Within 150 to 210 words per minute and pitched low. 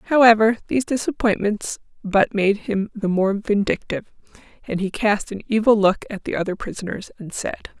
No: average, 160 wpm; high, 210 Hz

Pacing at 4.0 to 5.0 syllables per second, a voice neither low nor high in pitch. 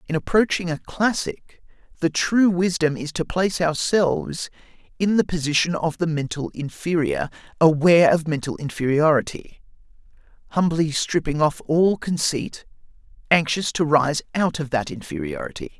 Yes: 4.8 syllables/s; medium, 160 Hz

